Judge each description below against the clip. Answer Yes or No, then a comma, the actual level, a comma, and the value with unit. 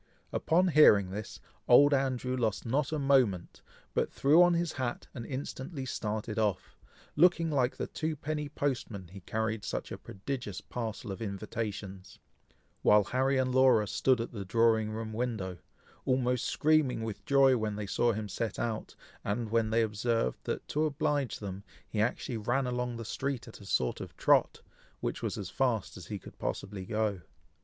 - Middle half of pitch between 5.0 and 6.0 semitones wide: No, average, 4.2 semitones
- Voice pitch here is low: Yes, low, 115 Hz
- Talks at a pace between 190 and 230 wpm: No, average, 170 wpm